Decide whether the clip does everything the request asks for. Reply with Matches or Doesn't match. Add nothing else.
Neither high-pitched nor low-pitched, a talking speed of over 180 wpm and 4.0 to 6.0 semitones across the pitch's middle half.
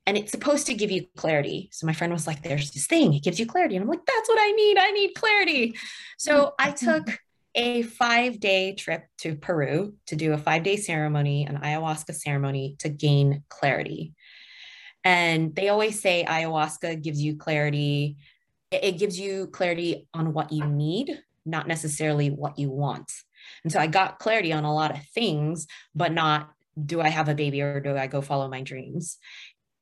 Matches